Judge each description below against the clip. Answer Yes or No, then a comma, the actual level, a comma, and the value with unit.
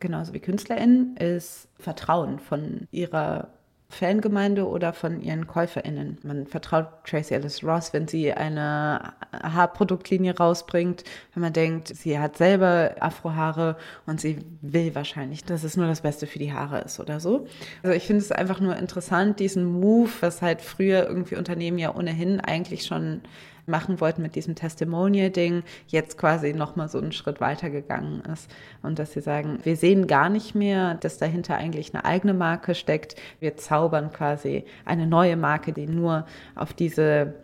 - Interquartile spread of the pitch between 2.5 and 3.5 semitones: Yes, average, 2.8 semitones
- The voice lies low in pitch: No, medium, 165 Hz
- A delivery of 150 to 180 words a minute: Yes, average, 165 wpm